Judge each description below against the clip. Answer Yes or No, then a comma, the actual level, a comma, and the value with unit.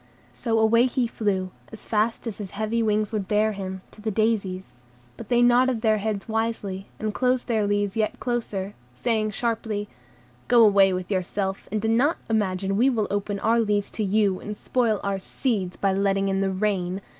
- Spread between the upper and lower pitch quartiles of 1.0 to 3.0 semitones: Yes, narrow, 2.4 semitones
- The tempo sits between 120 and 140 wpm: No, average, 190 wpm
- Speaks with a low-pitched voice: No, high, 210 Hz